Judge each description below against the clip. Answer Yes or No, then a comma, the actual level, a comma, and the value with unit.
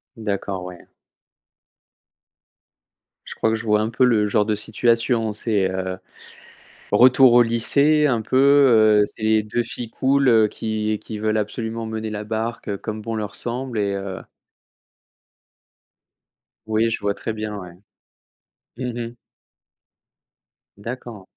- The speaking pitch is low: Yes, low, 110 Hz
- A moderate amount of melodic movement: No, narrow, 2.0 semitones